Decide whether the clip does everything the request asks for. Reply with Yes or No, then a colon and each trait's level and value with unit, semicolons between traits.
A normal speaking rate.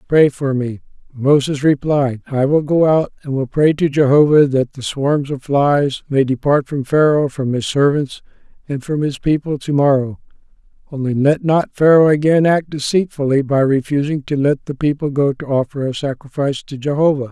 Yes: average, 180 wpm